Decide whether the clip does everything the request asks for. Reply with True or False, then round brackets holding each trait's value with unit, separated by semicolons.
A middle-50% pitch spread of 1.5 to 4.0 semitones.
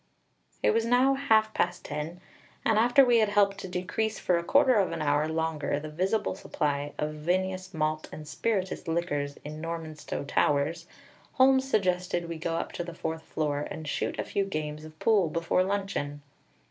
False (4.8 semitones)